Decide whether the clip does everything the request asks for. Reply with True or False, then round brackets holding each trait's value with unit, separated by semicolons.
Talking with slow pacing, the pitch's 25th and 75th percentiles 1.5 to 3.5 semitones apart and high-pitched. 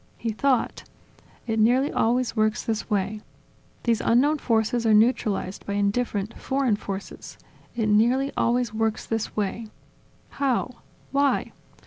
True (125 wpm; 2.7 semitones; 225 Hz)